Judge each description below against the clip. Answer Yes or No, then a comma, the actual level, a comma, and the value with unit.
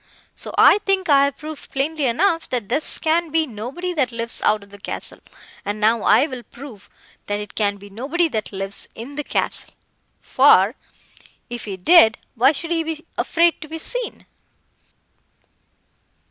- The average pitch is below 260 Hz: No, very high, 270 Hz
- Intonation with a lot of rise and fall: Yes, wide, 7.0 semitones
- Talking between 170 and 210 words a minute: No, average, 160 wpm